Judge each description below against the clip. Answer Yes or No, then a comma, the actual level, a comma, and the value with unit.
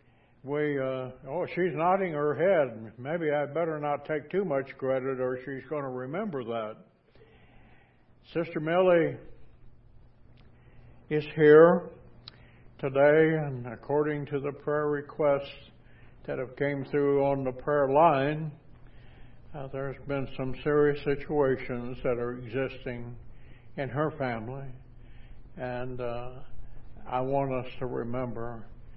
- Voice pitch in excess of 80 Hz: Yes, low, 135 Hz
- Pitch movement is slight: No, average, 3.0 semitones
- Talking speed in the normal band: No, slow, 120 wpm